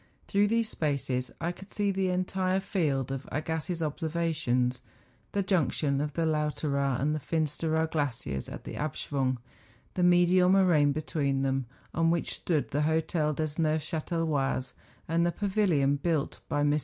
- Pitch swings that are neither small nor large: Yes, average, 3.6 semitones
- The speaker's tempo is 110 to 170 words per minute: Yes, average, 155 wpm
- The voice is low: No, medium, 155 Hz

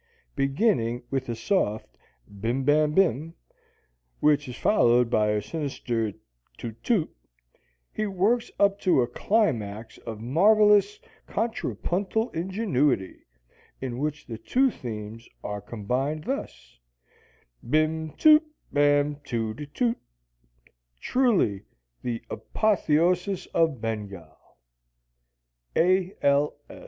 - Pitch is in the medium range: Yes, medium, 145 Hz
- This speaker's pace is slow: Yes, slow, 105 wpm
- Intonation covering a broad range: Yes, wide, 8.7 semitones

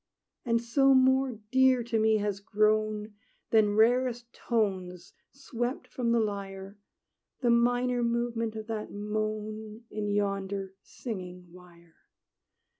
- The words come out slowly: Yes, slow, 115 wpm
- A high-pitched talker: Yes, high, 215 Hz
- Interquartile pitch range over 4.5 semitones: No, average, 2.8 semitones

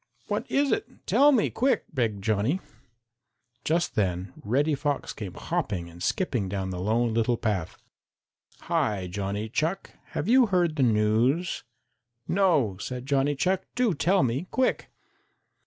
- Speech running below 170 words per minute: Yes, average, 140 wpm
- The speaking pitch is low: Yes, low, 125 Hz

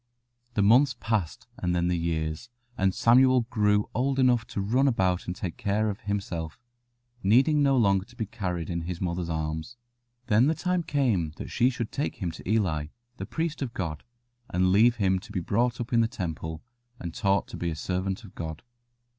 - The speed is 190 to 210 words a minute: Yes, average, 195 wpm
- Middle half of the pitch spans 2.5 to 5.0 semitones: No, wide, 5.5 semitones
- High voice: No, low, 100 Hz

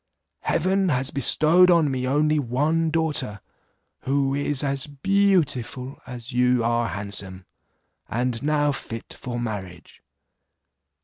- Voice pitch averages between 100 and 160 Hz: Yes, low, 135 Hz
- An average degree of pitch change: Yes, average, 4.2 semitones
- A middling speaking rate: No, slow, 115 wpm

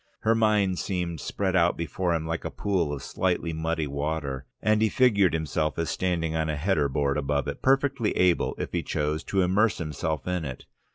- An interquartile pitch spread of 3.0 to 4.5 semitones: Yes, average, 4.0 semitones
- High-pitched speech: No, very low, 85 Hz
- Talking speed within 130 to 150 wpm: No, average, 195 wpm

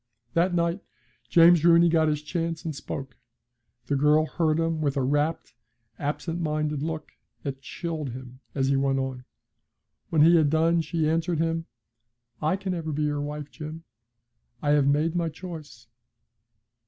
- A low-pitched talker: No, medium, 155 Hz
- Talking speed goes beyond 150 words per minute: Yes, average, 160 wpm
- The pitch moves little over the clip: Yes, narrow, 2.3 semitones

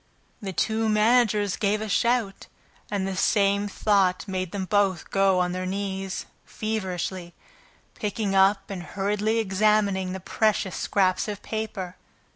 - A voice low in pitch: No, high, 200 Hz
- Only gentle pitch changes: Yes, narrow, 2.1 semitones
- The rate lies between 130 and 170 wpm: Yes, slow, 135 wpm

